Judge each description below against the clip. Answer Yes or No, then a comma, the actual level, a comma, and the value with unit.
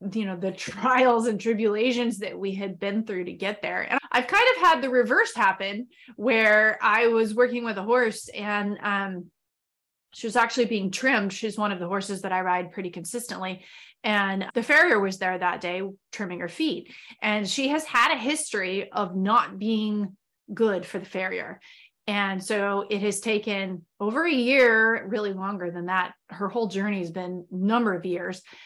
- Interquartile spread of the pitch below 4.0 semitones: Yes, average, 3.5 semitones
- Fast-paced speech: No, average, 185 wpm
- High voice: Yes, high, 205 Hz